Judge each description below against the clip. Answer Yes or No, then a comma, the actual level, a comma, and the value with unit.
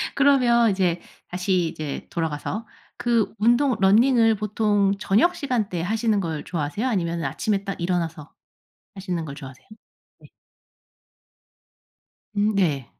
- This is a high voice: Yes, high, 195 Hz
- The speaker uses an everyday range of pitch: Yes, average, 4.9 semitones